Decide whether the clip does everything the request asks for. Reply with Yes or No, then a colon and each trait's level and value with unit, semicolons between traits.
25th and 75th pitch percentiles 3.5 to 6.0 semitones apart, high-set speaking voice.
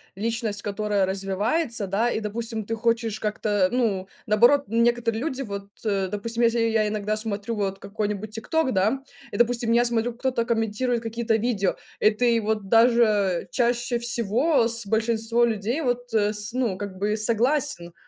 No: narrow, 2.5 semitones; high, 225 Hz